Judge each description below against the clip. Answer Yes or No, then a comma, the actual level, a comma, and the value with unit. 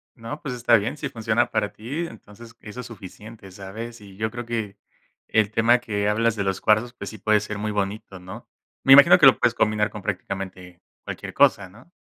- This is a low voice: Yes, low, 110 Hz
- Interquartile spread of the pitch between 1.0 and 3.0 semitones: Yes, average, 2.7 semitones